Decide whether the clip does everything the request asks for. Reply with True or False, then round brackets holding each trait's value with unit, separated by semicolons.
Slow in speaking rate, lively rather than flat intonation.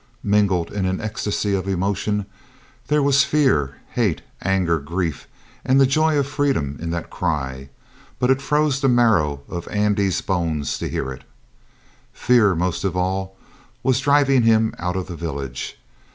False (155 wpm; 6.9 semitones)